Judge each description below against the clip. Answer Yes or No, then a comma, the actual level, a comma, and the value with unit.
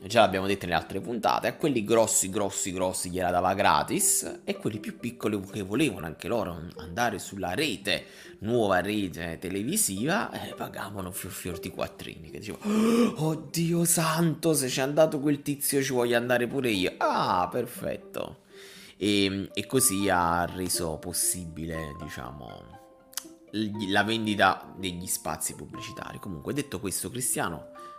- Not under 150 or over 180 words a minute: No, average, 140 wpm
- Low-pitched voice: Yes, low, 100 Hz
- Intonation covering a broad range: Yes, wide, 6.8 semitones